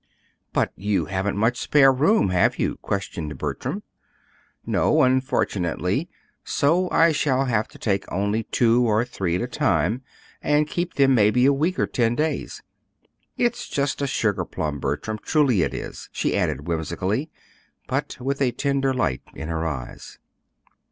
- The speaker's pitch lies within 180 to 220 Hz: No, low, 120 Hz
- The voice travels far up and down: Yes, wide, 6.5 semitones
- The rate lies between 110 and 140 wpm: No, average, 155 wpm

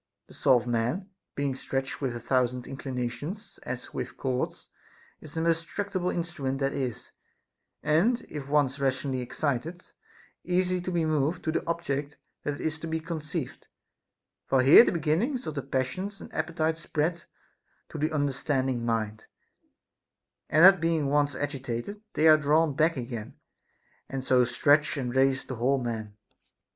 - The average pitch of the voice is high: No, medium, 145 Hz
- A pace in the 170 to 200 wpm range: No, average, 155 wpm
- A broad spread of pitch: No, average, 4.0 semitones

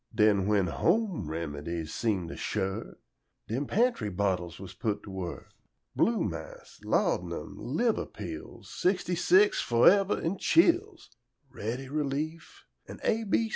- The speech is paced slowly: Yes, slow, 130 wpm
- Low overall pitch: Yes, low, 125 Hz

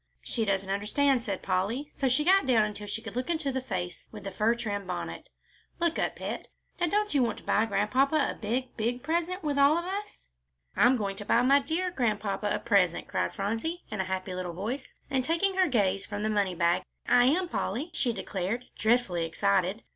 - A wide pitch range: Yes, wide, 6.2 semitones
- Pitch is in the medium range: No, high, 230 Hz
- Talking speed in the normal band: No, fast, 210 wpm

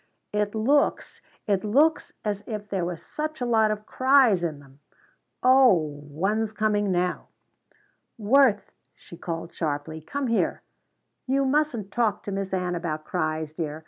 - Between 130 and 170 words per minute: Yes, average, 150 wpm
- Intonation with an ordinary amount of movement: No, wide, 6.0 semitones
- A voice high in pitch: Yes, high, 205 Hz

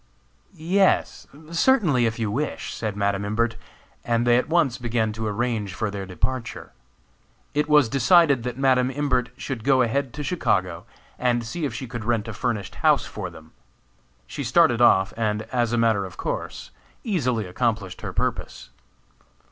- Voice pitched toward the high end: No, low, 120 Hz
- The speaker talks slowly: No, average, 165 wpm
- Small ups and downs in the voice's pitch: No, average, 3.8 semitones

